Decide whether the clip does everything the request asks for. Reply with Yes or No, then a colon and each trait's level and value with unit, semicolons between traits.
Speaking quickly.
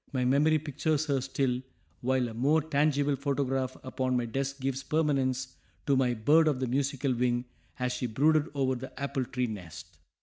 No: average, 175 wpm